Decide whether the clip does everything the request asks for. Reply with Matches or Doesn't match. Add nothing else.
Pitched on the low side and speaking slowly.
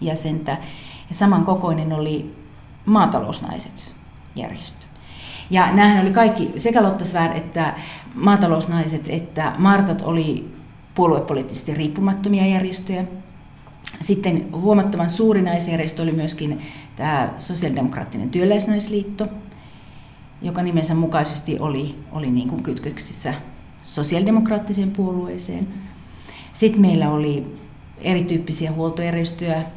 Doesn't match